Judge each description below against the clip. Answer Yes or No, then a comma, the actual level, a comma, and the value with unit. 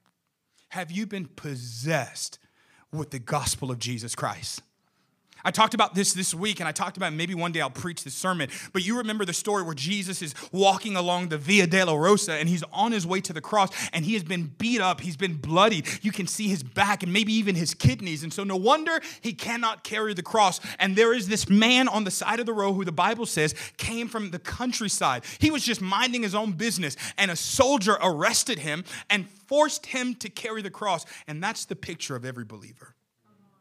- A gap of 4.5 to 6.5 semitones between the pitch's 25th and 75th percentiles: Yes, average, 4.8 semitones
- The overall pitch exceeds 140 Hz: Yes, high, 190 Hz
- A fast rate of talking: Yes, fast, 220 wpm